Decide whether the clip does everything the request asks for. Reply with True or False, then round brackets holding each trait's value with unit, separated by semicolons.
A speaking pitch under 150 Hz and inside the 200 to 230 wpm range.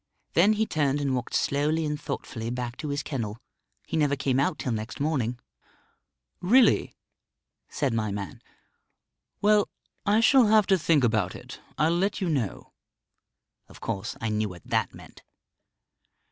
False (140 Hz; 155 wpm)